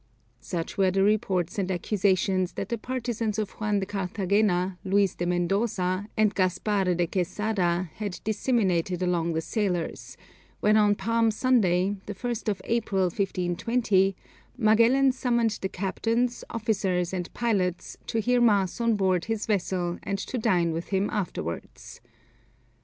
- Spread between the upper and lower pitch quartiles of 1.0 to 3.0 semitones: No, average, 3.4 semitones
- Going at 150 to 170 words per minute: No, average, 140 wpm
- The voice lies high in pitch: Yes, high, 200 Hz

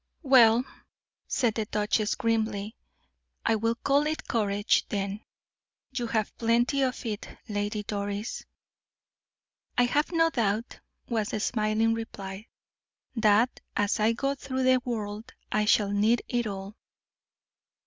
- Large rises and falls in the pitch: No, average, 2.7 semitones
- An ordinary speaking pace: No, slow, 130 wpm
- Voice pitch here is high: Yes, high, 225 Hz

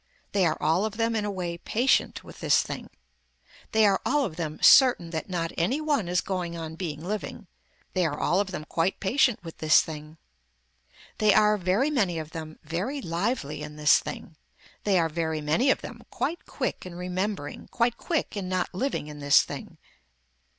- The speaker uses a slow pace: No, average, 190 wpm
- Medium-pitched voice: Yes, medium, 180 Hz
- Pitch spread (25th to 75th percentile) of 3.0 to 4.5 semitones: No, average, 4.9 semitones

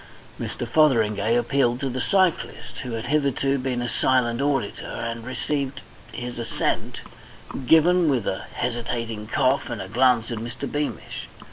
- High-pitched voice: No, low, 125 Hz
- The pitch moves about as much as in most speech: Yes, average, 3.0 semitones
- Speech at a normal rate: Yes, average, 145 wpm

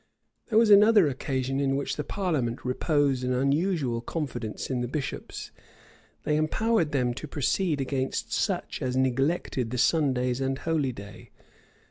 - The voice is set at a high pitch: No, low, 135 Hz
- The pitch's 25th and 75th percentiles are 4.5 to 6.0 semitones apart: No, average, 3.8 semitones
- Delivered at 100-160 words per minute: Yes, average, 150 wpm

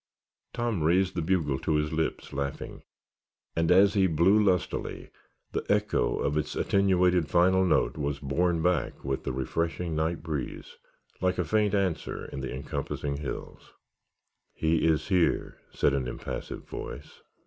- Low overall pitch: Yes, very low, 85 Hz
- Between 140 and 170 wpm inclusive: Yes, average, 150 wpm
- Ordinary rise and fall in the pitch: Yes, average, 3.8 semitones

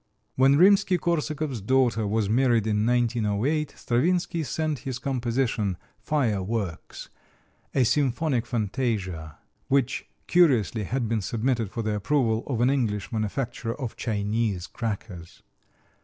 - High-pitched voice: No, low, 120 Hz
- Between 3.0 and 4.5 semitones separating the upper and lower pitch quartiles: Yes, average, 4.1 semitones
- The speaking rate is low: Yes, slow, 120 wpm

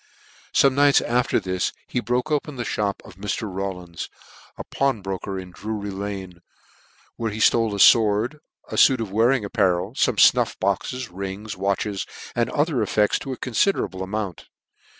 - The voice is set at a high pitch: No, low, 105 Hz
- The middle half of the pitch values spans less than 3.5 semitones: No, average, 4.1 semitones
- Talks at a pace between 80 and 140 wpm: No, average, 160 wpm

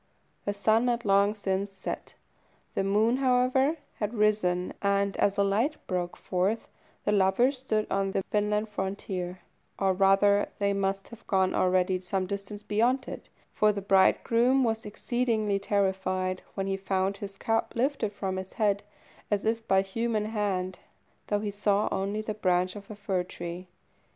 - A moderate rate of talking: Yes, average, 160 wpm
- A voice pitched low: No, high, 200 Hz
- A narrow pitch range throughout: Yes, narrow, 2.1 semitones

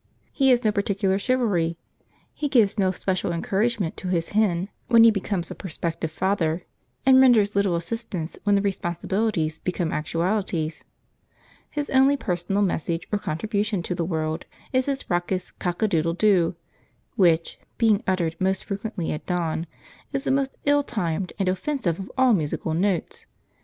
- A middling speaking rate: Yes, average, 155 wpm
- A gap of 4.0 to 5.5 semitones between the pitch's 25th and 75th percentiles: Yes, average, 4.3 semitones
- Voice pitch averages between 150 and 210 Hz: Yes, high, 190 Hz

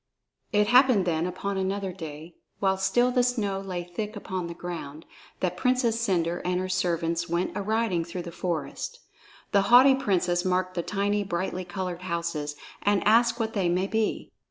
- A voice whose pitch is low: No, medium, 185 Hz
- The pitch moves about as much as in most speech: Yes, average, 3.1 semitones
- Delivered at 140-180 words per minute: Yes, average, 175 wpm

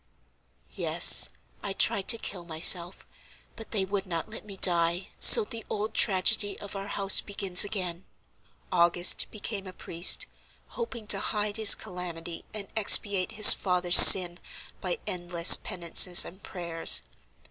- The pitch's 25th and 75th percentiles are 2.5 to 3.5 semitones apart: Yes, average, 2.9 semitones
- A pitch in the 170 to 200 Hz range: Yes, high, 190 Hz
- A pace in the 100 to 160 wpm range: Yes, average, 140 wpm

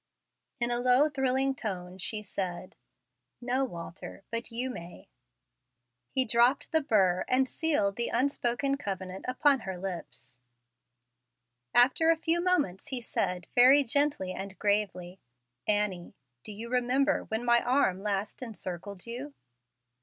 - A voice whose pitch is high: Yes, high, 235 Hz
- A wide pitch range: Yes, wide, 5.7 semitones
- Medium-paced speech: No, slow, 130 wpm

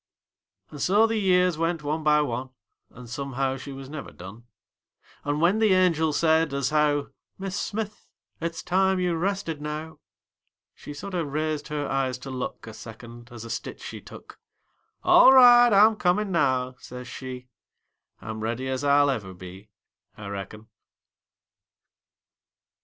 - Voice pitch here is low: No, medium, 150 Hz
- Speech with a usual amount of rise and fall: No, wide, 6.1 semitones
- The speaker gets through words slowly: No, average, 150 wpm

